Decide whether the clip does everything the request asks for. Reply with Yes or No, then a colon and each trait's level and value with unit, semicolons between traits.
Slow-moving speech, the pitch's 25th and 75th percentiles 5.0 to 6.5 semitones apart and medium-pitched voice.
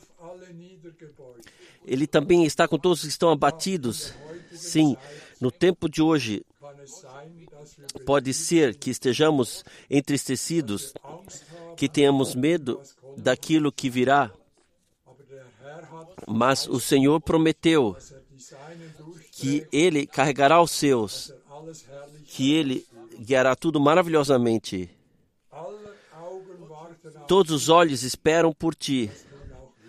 No: slow, 90 wpm; average, 3.6 semitones; medium, 150 Hz